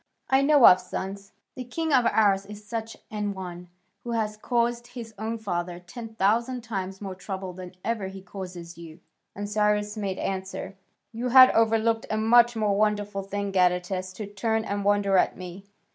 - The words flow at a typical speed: Yes, average, 175 wpm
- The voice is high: Yes, high, 205 Hz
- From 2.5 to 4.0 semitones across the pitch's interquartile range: Yes, average, 3.0 semitones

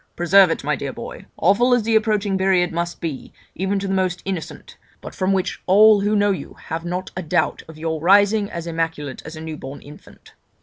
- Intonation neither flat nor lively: Yes, average, 3.6 semitones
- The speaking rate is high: Yes, fast, 215 wpm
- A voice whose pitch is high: No, medium, 180 Hz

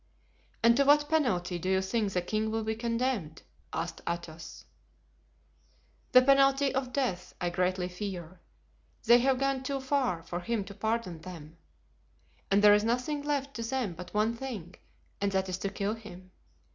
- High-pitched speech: Yes, high, 215 Hz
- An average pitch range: No, wide, 6.1 semitones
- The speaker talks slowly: No, average, 170 wpm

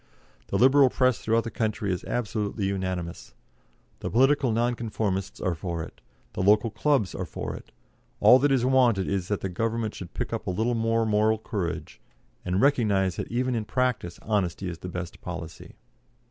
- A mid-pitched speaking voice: No, low, 110 Hz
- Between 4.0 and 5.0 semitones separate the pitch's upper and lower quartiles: Yes, average, 4.4 semitones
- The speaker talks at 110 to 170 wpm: No, average, 180 wpm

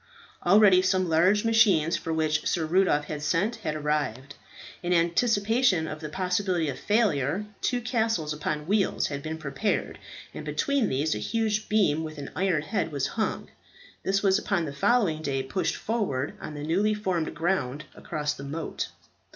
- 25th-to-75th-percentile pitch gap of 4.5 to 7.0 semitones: Yes, average, 5.3 semitones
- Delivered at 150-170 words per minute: Yes, average, 165 wpm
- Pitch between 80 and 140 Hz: No, medium, 170 Hz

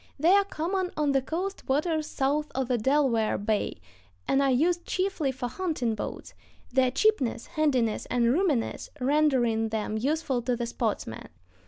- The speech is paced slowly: No, average, 155 wpm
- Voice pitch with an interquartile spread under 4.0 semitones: No, average, 4.7 semitones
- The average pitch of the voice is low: No, very high, 270 Hz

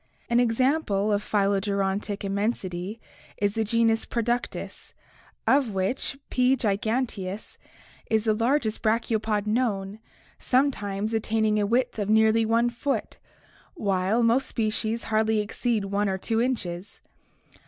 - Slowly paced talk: Yes, slow, 115 wpm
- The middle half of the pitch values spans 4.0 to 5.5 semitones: No, narrow, 2.6 semitones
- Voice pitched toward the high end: Yes, high, 220 Hz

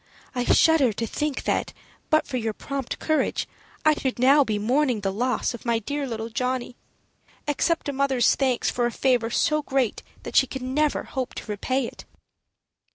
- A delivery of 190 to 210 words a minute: No, average, 180 wpm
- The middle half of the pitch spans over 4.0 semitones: No, average, 3.2 semitones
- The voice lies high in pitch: Yes, very high, 255 Hz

